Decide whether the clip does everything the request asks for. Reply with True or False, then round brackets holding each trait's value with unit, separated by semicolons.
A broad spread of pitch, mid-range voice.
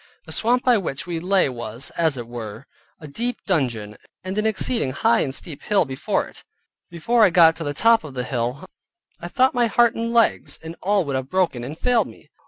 True (8.4 semitones; 165 Hz)